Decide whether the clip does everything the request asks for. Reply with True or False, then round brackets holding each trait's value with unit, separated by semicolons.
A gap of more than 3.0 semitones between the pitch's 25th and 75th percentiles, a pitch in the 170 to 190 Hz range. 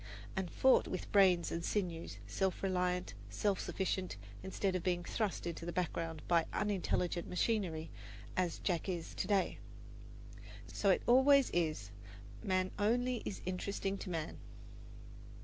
False (2.7 semitones; 185 Hz)